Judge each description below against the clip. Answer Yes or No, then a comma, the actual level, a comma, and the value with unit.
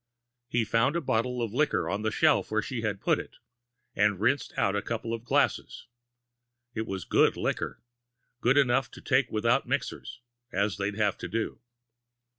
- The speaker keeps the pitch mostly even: No, average, 3.0 semitones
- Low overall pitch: Yes, low, 115 Hz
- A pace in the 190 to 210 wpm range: No, average, 175 wpm